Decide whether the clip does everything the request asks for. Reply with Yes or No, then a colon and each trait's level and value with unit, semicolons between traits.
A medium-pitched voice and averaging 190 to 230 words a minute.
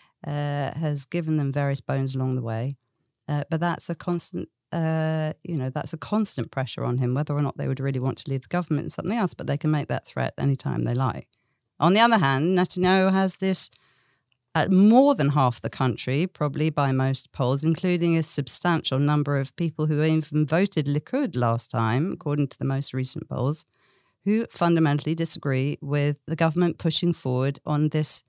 Yes: medium, 150 Hz; average, 195 wpm